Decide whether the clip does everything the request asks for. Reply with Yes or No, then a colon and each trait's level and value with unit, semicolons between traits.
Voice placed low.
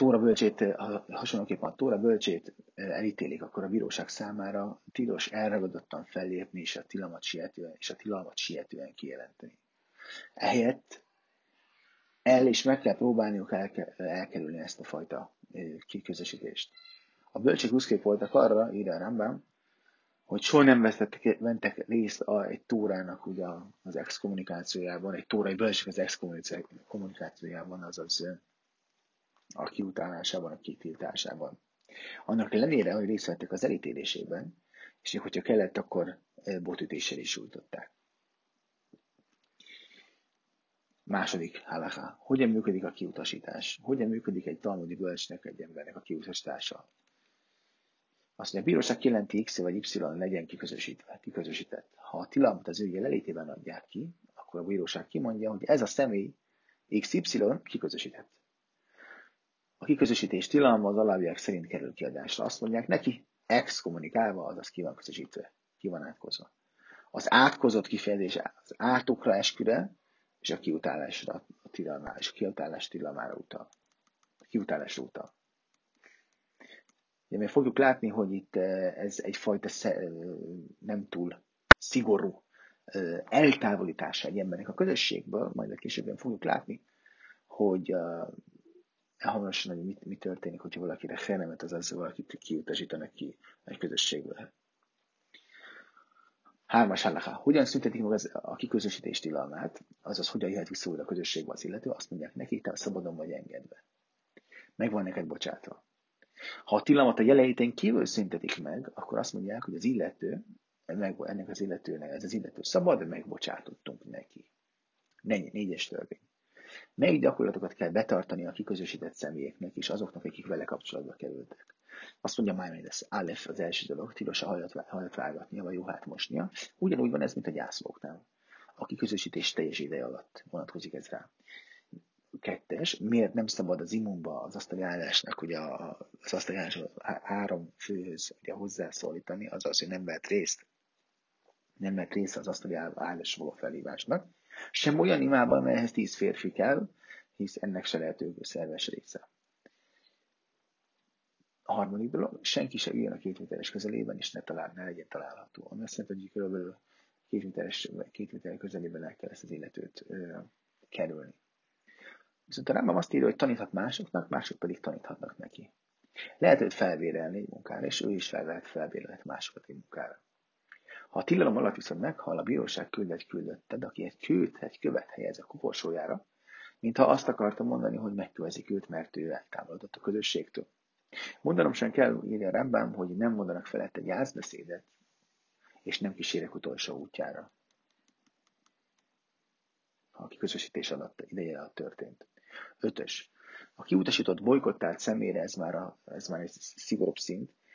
Yes: low, 105 Hz